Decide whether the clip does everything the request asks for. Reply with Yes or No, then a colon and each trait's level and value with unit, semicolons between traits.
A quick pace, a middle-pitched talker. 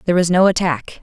Yes: fast, 235 wpm; medium, 175 Hz